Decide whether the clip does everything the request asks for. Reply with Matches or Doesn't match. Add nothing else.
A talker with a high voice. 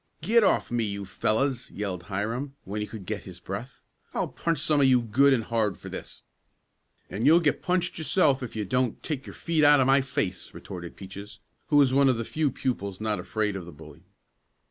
Doesn't match